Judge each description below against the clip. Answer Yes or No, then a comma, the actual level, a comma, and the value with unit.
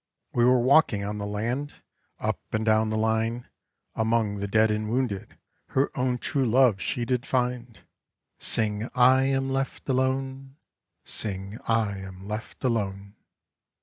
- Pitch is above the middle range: No, low, 115 Hz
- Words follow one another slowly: No, average, 145 wpm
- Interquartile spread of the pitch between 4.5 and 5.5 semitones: No, average, 3.5 semitones